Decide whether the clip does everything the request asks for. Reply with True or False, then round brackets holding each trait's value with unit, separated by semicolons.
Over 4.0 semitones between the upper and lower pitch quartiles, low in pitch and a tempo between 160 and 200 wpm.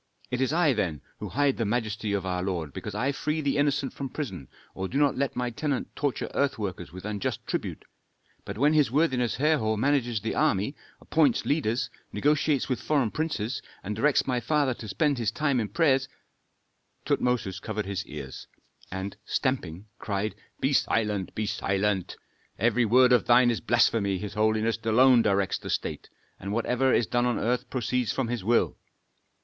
True (4.7 semitones; 120 Hz; 180 wpm)